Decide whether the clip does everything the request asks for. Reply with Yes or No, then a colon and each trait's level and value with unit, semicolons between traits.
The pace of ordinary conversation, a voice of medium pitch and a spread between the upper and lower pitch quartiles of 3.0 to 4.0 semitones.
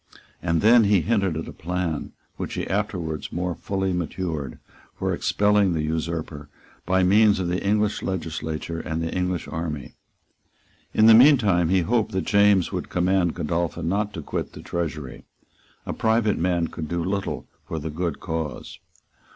No: average, 160 wpm; very low, 90 Hz; average, 3.6 semitones